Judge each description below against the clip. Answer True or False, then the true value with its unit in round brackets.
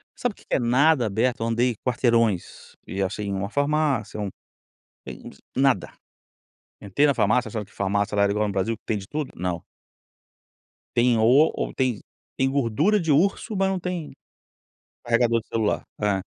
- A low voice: True (115 Hz)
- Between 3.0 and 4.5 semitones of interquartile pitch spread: False (5.6 semitones)